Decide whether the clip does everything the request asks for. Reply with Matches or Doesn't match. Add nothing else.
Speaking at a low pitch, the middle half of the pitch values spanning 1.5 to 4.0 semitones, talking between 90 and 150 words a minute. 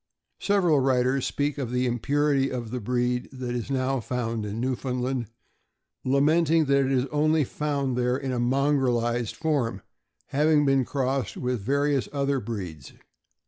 Matches